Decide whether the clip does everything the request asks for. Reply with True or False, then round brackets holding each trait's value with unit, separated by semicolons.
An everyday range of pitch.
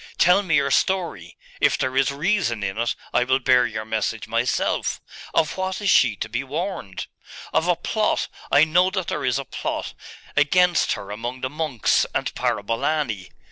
False (7.1 semitones)